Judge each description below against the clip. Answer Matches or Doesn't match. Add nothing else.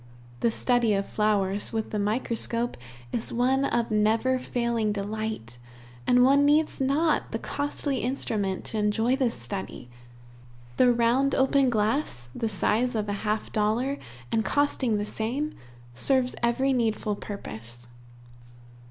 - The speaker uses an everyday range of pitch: Matches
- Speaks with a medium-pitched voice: Doesn't match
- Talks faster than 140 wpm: Doesn't match